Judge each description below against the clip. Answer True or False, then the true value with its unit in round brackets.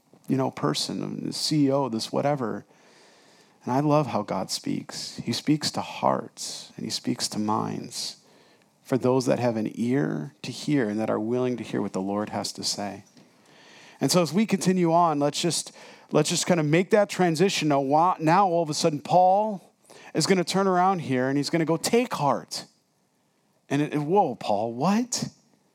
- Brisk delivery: False (195 wpm)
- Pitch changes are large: True (6.9 semitones)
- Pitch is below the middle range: False (150 Hz)